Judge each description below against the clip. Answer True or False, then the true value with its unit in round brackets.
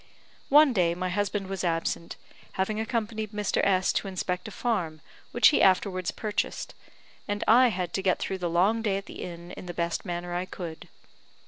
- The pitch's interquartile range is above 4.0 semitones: False (3.2 semitones)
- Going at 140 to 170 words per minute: False (190 wpm)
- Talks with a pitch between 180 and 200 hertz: True (190 Hz)